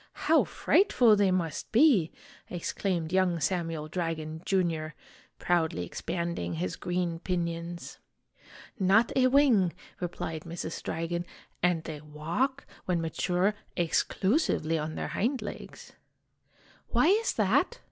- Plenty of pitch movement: No, average, 3.3 semitones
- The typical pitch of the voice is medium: Yes, medium, 175 Hz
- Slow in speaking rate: Yes, slow, 115 wpm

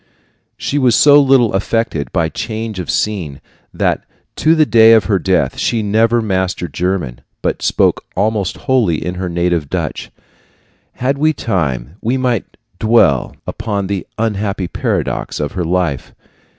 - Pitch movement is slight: No, average, 4.7 semitones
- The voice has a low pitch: Yes, low, 100 Hz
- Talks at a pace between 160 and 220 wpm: No, average, 150 wpm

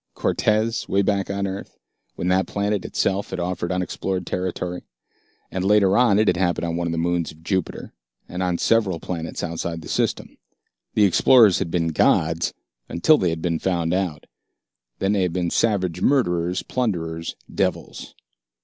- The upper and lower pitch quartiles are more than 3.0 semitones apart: No, average, 2.7 semitones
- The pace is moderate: Yes, average, 165 wpm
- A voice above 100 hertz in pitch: No, very low, 90 Hz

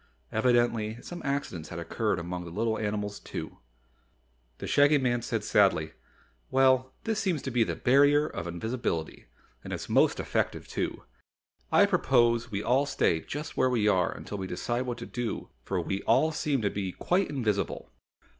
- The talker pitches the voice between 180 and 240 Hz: No, low, 120 Hz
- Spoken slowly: No, average, 170 wpm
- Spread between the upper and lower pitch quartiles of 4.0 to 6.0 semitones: Yes, average, 4.8 semitones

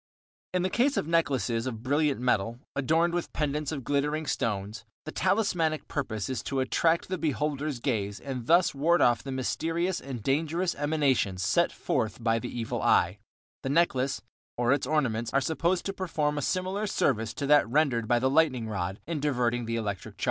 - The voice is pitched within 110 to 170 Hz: Yes, medium, 140 Hz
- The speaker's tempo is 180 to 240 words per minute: Yes, average, 185 wpm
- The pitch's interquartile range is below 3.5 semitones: No, average, 5.3 semitones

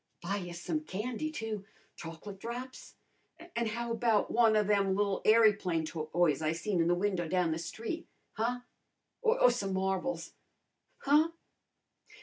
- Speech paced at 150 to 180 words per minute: No, average, 140 wpm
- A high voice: Yes, high, 205 Hz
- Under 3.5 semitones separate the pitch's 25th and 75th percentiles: No, average, 5.1 semitones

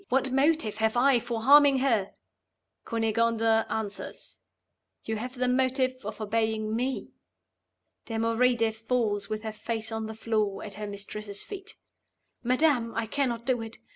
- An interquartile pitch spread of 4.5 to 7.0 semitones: No, narrow, 2.6 semitones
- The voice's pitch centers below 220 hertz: No, high, 230 Hz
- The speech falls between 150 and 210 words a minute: No, average, 140 wpm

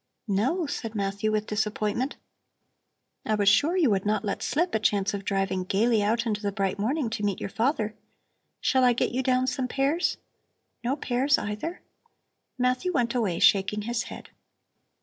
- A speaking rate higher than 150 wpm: Yes, average, 170 wpm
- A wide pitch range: No, average, 4.0 semitones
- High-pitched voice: Yes, high, 220 Hz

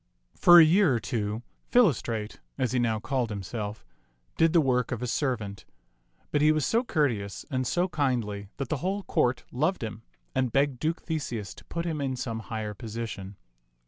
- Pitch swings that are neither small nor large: No, wide, 5.7 semitones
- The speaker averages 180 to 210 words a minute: Yes, average, 185 wpm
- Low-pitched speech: Yes, low, 125 Hz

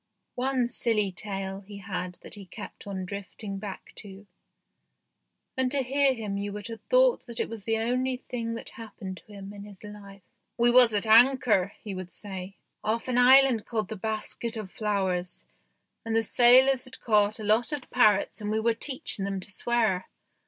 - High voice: Yes, high, 215 Hz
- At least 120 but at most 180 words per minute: No, average, 190 wpm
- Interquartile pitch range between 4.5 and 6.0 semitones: No, average, 3.4 semitones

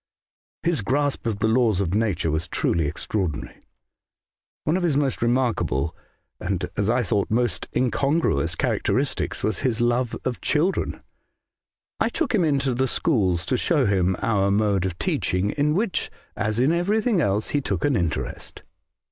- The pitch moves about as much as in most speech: No, wide, 6.6 semitones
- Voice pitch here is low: Yes, low, 115 Hz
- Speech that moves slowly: No, average, 165 wpm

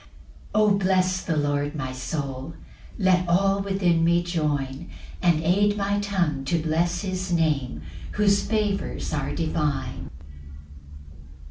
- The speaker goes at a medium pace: No, slow, 125 wpm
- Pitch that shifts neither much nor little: Yes, average, 4.5 semitones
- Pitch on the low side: No, medium, 170 Hz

